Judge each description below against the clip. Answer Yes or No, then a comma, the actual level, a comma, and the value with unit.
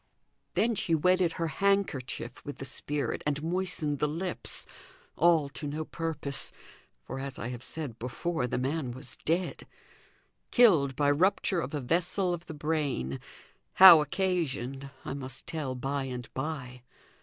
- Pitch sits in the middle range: Yes, medium, 150 Hz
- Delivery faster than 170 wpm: No, average, 150 wpm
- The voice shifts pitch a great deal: No, average, 4.2 semitones